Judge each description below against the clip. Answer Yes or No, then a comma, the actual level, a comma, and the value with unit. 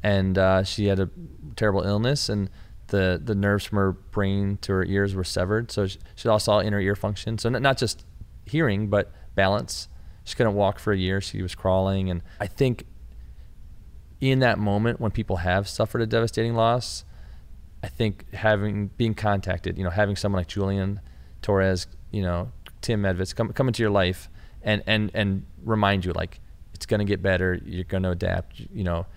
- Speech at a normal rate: Yes, average, 190 wpm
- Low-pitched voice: Yes, low, 100 Hz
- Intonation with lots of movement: No, narrow, 2.5 semitones